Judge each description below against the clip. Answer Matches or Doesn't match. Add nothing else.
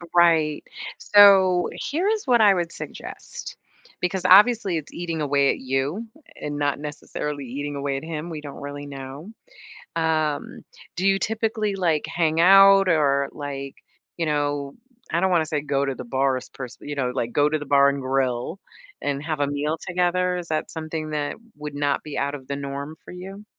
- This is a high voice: Doesn't match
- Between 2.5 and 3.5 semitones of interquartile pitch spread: Doesn't match